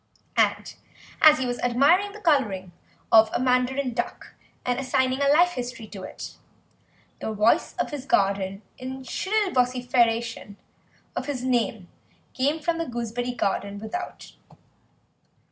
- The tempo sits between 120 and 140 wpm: Yes, slow, 135 wpm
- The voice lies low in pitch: No, very high, 250 Hz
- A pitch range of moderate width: Yes, average, 3.8 semitones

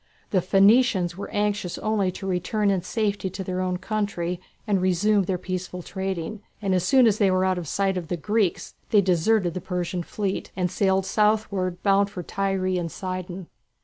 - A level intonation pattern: Yes, narrow, 2.1 semitones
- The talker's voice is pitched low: No, high, 190 Hz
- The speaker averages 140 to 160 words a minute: No, average, 185 wpm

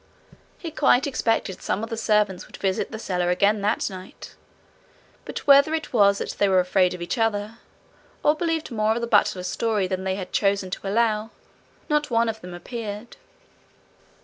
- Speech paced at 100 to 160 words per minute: No, average, 180 wpm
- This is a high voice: Yes, high, 210 Hz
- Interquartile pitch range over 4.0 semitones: No, average, 3.6 semitones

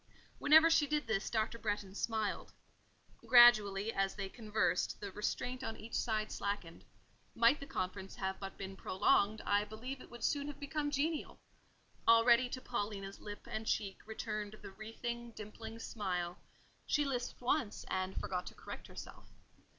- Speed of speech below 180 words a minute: Yes, average, 155 wpm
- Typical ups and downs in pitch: Yes, average, 3.5 semitones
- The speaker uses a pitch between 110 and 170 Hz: No, high, 220 Hz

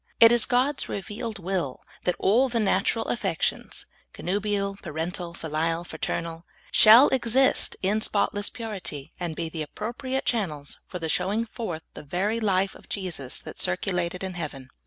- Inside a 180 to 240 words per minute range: No, average, 155 wpm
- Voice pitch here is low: No, high, 190 Hz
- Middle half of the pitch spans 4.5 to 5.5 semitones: Yes, average, 5.0 semitones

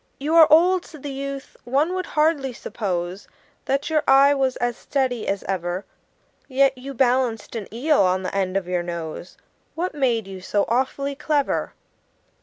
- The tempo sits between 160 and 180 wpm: Yes, average, 170 wpm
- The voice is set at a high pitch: Yes, very high, 260 Hz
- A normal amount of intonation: No, wide, 6.3 semitones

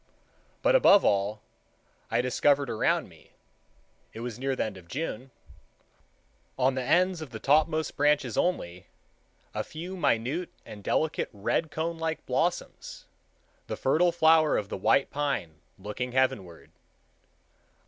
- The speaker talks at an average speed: No, slow, 125 wpm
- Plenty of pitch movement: Yes, wide, 6.7 semitones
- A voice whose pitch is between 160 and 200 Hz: No, low, 135 Hz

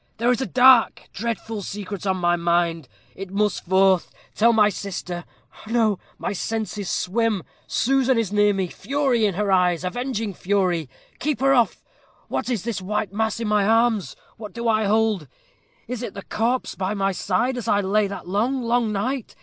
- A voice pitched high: Yes, high, 210 Hz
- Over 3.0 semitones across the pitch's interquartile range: Yes, average, 3.4 semitones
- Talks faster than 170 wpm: Yes, average, 180 wpm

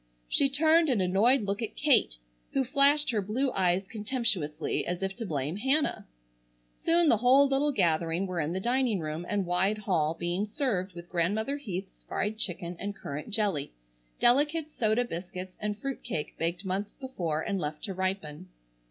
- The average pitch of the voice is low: No, high, 200 Hz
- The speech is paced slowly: No, average, 170 wpm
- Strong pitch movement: Yes, wide, 6.3 semitones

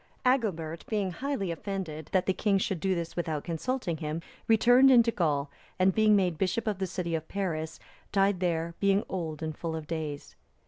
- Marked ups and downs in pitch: No, average, 3.9 semitones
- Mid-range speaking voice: Yes, medium, 180 Hz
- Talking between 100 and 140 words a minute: No, average, 190 wpm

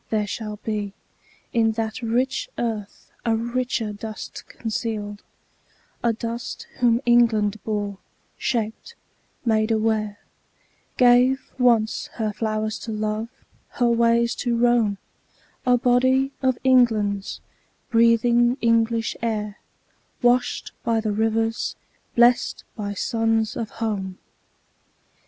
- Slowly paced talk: Yes, slow, 105 wpm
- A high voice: Yes, high, 225 Hz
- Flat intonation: Yes, narrow, 1.8 semitones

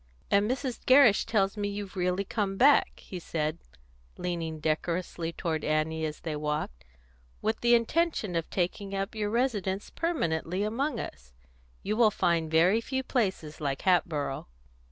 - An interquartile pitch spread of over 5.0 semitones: Yes, wide, 5.4 semitones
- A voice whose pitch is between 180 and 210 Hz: Yes, high, 190 Hz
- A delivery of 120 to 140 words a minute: No, average, 155 wpm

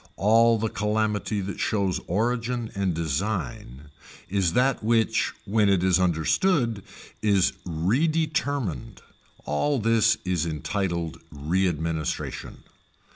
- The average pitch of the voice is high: No, low, 100 Hz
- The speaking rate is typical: No, slow, 100 wpm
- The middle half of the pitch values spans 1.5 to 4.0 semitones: No, average, 5.1 semitones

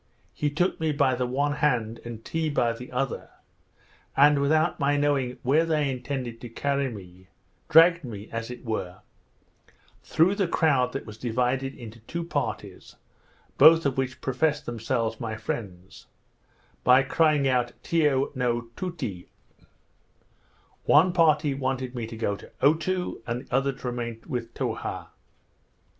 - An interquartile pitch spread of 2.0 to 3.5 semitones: No, average, 4.0 semitones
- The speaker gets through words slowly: No, average, 150 wpm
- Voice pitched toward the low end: Yes, low, 130 Hz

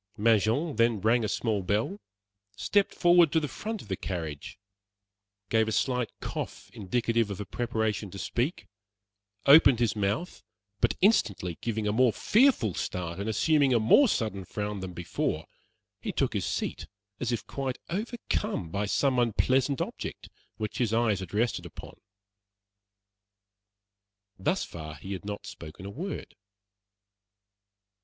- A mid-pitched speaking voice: No, low, 110 Hz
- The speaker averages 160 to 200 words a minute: No, average, 145 wpm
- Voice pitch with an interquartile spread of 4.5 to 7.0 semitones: Yes, average, 5.2 semitones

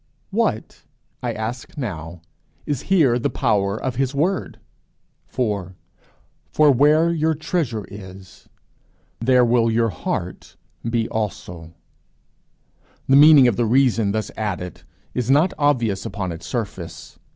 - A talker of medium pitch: No, low, 115 Hz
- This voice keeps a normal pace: No, slow, 125 wpm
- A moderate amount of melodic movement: No, wide, 5.7 semitones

